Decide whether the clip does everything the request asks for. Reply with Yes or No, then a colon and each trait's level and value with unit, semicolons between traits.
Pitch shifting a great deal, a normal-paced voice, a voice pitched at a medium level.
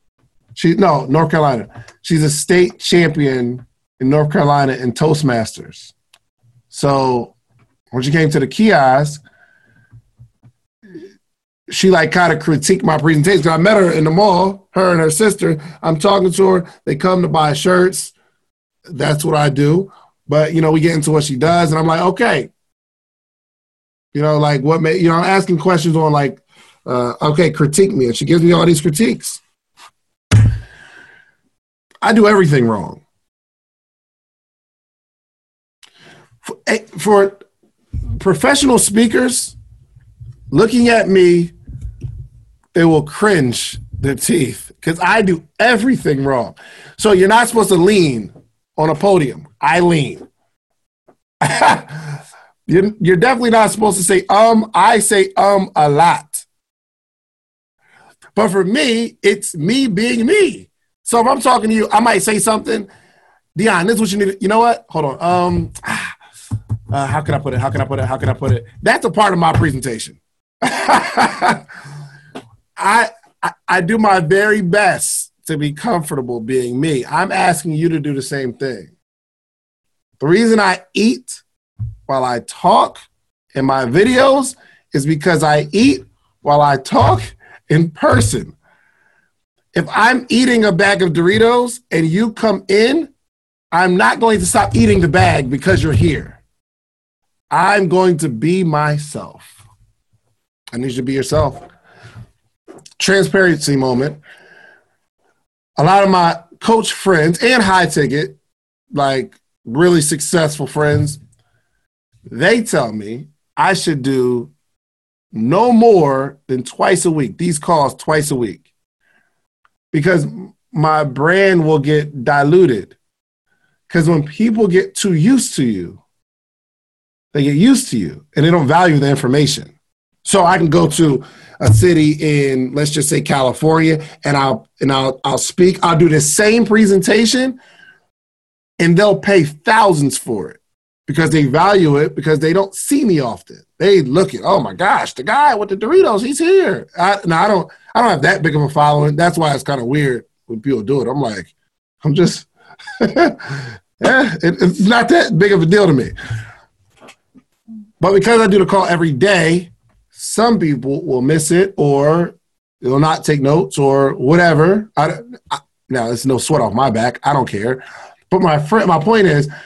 Yes: wide, 6.2 semitones; average, 155 wpm; medium, 160 Hz